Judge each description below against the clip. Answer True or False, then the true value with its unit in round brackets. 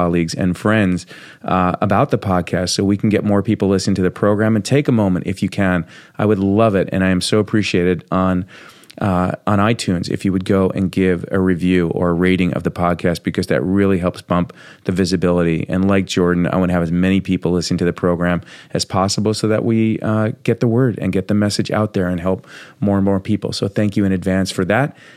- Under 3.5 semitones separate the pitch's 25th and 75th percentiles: True (2.5 semitones)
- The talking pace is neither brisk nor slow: False (240 wpm)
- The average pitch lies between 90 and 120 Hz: True (95 Hz)